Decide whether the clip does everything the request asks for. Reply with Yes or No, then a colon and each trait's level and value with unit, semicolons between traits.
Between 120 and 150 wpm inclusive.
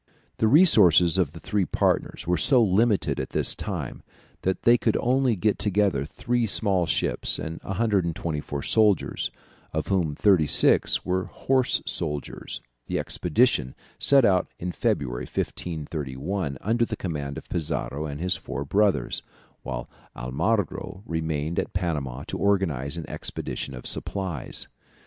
Yes: average, 140 wpm